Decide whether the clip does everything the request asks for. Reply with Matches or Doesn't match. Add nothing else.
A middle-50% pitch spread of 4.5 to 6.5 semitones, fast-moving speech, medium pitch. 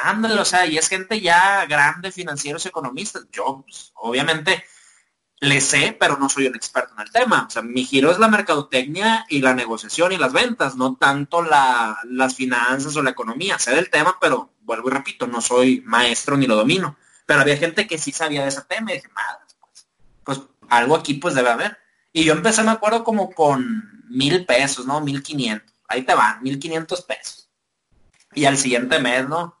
Matches